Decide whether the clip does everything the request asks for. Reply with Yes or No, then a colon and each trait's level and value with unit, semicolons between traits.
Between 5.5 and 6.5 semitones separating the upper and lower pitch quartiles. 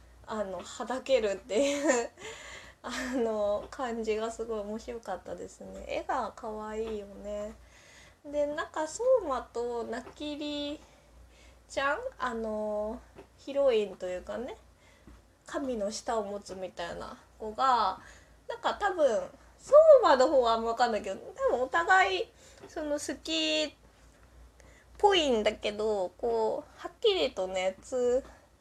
Yes: wide, 6.1 semitones